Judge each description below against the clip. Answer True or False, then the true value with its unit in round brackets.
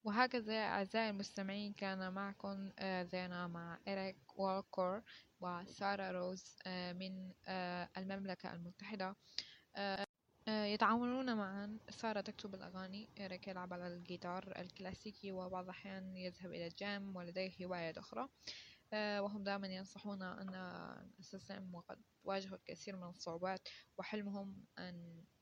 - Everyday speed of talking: True (105 wpm)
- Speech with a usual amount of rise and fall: False (1.6 semitones)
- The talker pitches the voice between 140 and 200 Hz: True (190 Hz)